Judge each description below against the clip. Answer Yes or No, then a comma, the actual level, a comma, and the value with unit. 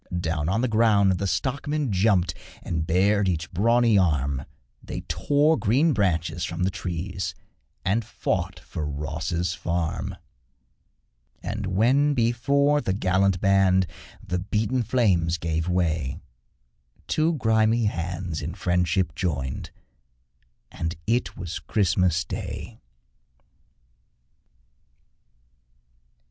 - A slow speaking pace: Yes, slow, 105 wpm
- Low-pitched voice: Yes, very low, 95 Hz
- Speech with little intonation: No, average, 5.0 semitones